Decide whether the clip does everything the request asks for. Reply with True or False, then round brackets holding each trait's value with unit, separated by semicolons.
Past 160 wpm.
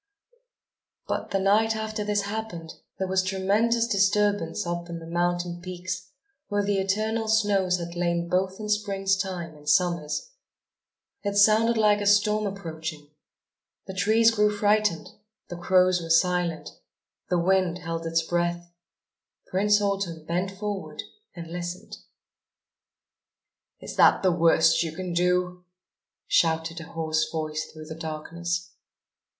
False (135 wpm)